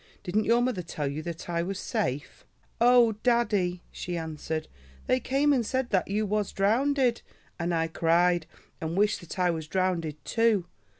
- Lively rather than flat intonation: Yes, wide, 5.7 semitones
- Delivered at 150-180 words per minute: Yes, average, 170 wpm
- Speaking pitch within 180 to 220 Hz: Yes, medium, 185 Hz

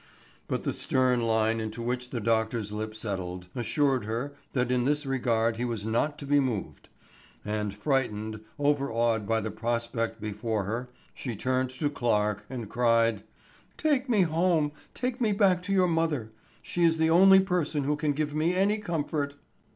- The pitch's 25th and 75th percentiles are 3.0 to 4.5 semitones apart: No, wide, 5.4 semitones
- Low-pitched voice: Yes, low, 125 Hz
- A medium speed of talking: Yes, average, 170 wpm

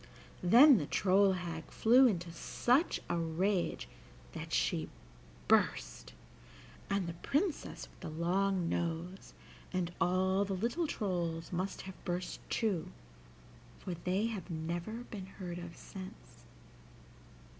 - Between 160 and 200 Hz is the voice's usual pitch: Yes, medium, 185 Hz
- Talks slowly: Yes, slow, 125 wpm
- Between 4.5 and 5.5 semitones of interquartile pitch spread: No, average, 2.9 semitones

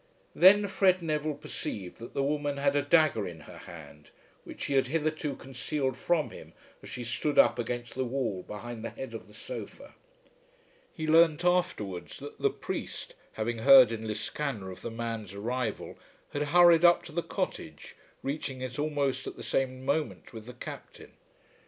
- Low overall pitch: Yes, low, 130 Hz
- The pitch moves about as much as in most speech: Yes, average, 5.0 semitones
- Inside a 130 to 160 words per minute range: No, average, 175 wpm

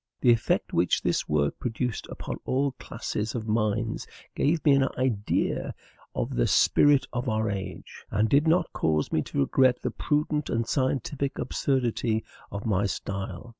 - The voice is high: No, low, 115 Hz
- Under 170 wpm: Yes, average, 160 wpm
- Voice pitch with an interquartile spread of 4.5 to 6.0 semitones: Yes, average, 4.8 semitones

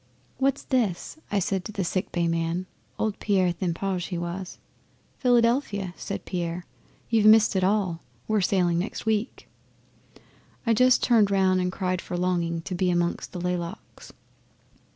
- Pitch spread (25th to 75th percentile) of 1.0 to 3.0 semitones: No, average, 3.5 semitones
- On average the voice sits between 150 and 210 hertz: Yes, medium, 185 Hz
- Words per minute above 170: No, average, 150 wpm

